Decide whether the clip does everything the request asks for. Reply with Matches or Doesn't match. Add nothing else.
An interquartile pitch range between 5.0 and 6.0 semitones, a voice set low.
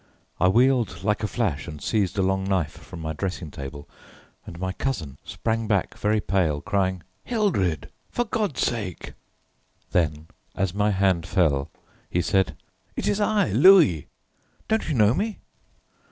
Matches